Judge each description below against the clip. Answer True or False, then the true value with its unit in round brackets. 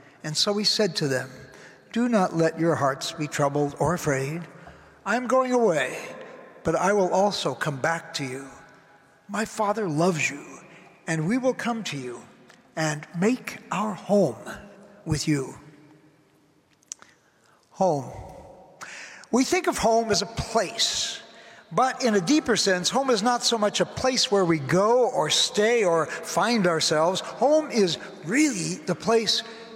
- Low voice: False (190 Hz)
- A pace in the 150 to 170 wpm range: True (155 wpm)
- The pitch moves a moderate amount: False (6.5 semitones)